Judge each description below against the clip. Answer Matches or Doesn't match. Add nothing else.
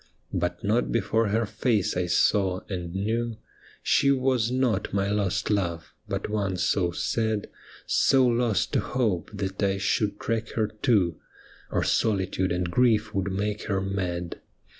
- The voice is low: Matches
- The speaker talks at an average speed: Matches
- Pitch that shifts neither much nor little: Matches